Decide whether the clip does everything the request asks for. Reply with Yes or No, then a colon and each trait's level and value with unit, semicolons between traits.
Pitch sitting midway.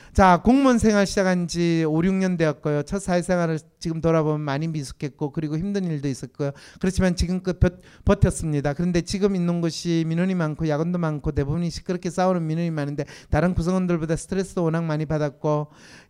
Yes: medium, 165 Hz